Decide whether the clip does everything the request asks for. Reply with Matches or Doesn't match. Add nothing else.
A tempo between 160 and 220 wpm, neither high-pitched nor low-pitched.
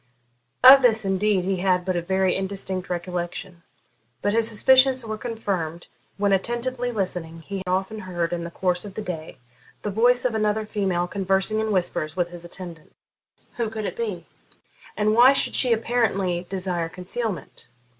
Doesn't match